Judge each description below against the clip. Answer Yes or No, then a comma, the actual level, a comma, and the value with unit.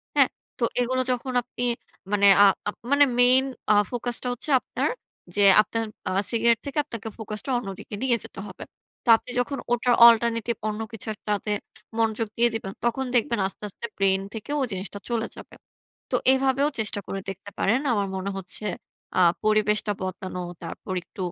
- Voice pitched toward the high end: Yes, high, 225 Hz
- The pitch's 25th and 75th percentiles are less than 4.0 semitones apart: Yes, average, 3.3 semitones